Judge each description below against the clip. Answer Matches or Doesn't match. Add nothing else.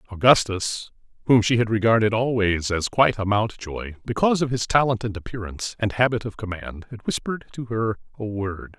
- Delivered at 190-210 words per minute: Doesn't match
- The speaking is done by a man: Matches